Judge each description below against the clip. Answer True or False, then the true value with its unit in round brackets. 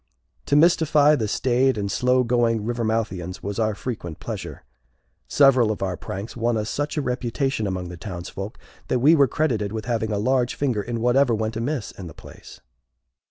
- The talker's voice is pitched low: True (115 Hz)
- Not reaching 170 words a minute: False (180 wpm)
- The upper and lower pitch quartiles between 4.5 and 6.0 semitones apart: False (3.9 semitones)